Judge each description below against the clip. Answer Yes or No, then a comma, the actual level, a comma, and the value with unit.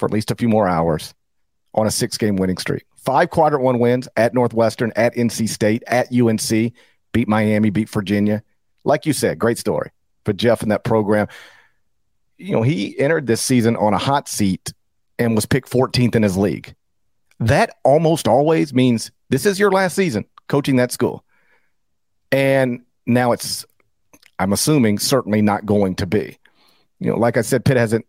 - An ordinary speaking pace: Yes, average, 180 wpm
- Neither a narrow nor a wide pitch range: Yes, average, 3.2 semitones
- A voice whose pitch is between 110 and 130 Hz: Yes, low, 115 Hz